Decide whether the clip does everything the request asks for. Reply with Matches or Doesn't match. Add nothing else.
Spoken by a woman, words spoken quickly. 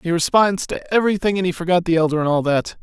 Doesn't match